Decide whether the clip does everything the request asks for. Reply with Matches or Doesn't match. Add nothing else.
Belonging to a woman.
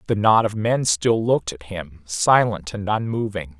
Doesn't match